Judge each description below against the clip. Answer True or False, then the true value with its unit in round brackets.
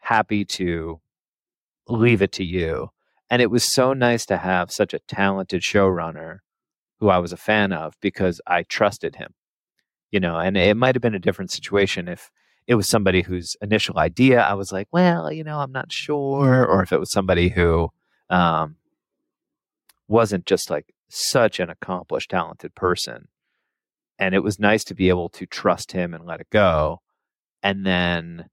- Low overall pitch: True (100 Hz)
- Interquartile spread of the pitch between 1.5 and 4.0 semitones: False (4.4 semitones)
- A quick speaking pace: False (175 wpm)